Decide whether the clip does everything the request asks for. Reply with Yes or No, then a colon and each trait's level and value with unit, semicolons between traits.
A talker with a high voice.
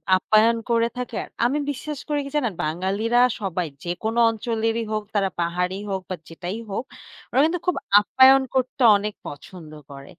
Yes: high, 215 Hz